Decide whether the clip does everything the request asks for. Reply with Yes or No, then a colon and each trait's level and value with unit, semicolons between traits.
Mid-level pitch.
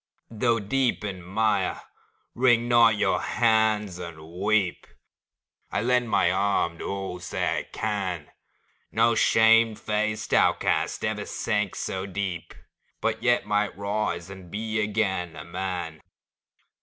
No: low, 105 Hz